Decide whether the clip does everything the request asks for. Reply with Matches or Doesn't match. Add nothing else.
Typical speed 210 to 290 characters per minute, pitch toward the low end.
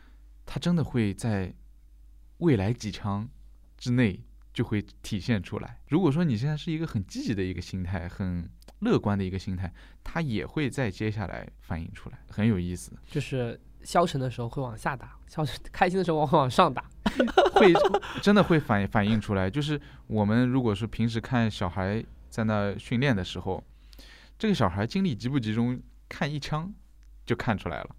Matches